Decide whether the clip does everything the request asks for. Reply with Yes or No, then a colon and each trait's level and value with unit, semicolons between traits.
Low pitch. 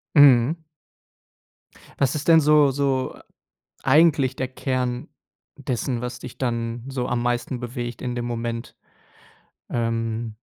Yes: low, 125 Hz